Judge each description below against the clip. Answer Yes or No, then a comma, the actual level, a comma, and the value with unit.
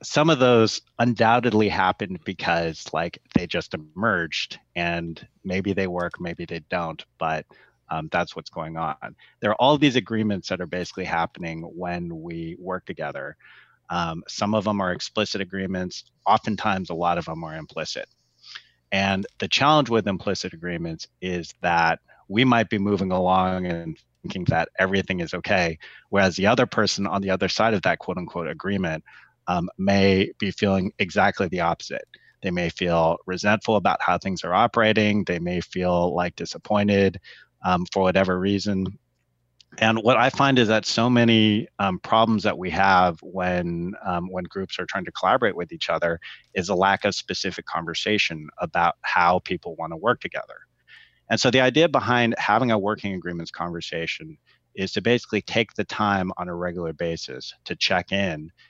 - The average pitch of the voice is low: Yes, very low, 95 Hz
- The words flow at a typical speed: Yes, average, 170 wpm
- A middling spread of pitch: Yes, average, 3.6 semitones